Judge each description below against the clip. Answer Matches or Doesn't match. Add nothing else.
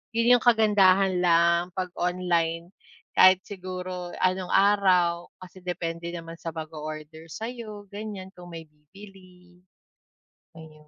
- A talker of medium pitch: Matches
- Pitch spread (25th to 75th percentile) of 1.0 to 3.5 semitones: Matches